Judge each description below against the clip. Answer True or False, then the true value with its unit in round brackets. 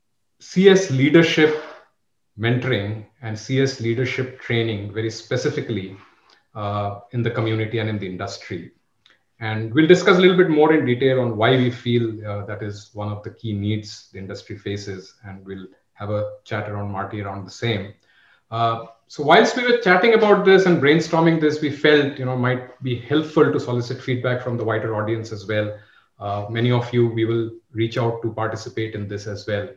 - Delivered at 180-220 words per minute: True (185 wpm)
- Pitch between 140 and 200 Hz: False (115 Hz)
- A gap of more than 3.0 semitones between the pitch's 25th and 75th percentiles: True (3.8 semitones)